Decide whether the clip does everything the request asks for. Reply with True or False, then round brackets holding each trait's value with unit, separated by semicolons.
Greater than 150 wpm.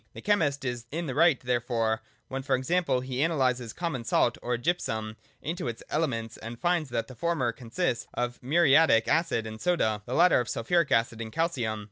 True (185 wpm)